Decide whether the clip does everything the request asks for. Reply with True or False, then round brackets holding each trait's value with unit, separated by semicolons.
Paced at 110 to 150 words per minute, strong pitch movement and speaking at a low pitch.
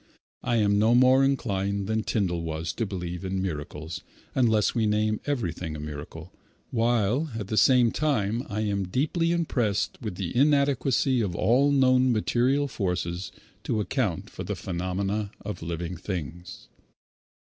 True (145 wpm; 5.7 semitones; 105 Hz)